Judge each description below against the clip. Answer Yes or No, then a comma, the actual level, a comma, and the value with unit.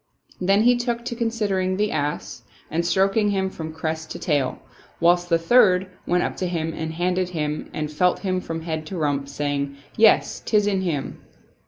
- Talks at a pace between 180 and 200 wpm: Yes, average, 185 wpm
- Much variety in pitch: No, average, 3.7 semitones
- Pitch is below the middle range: No, medium, 180 Hz